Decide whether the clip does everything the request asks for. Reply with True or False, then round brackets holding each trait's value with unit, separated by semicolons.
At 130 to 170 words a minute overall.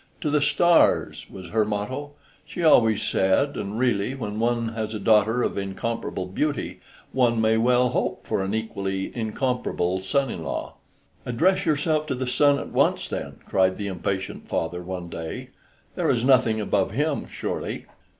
True (165 wpm)